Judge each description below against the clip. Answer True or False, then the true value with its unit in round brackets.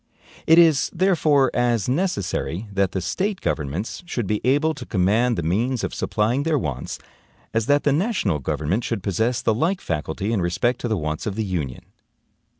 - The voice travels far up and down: True (7.3 semitones)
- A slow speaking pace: False (180 wpm)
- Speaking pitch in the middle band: False (115 Hz)